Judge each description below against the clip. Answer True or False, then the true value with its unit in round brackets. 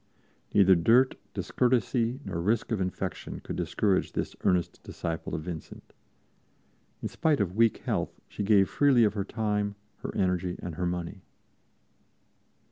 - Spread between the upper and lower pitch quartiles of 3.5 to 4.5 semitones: True (4.2 semitones)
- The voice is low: True (100 Hz)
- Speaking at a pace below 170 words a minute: True (140 wpm)